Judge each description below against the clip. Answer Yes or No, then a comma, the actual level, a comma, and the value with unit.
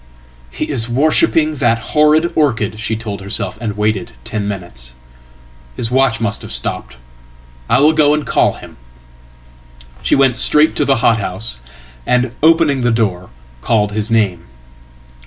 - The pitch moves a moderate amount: No, wide, 6.6 semitones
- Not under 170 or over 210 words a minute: No, average, 140 wpm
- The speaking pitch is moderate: No, low, 110 Hz